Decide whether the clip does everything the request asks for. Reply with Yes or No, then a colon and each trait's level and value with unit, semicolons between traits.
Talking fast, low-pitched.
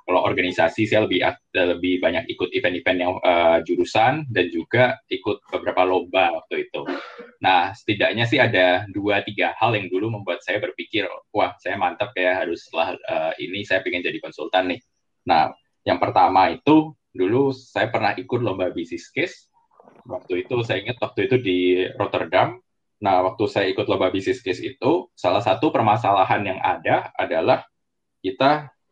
Yes: fast, 160 wpm; low, 125 Hz